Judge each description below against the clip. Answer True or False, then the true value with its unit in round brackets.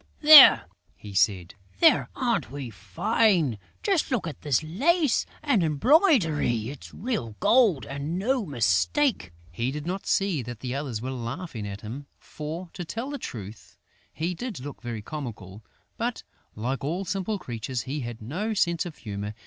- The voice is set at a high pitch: False (145 Hz)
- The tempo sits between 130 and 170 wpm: True (160 wpm)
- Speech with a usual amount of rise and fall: False (9.0 semitones)